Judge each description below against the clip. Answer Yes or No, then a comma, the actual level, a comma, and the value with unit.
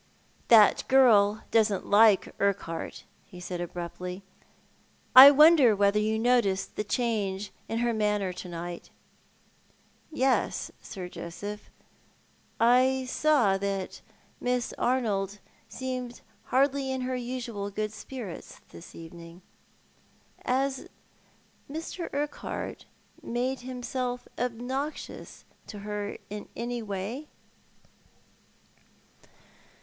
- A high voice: Yes, high, 225 Hz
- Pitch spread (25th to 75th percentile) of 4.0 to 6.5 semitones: Yes, average, 4.3 semitones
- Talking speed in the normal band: No, slow, 100 wpm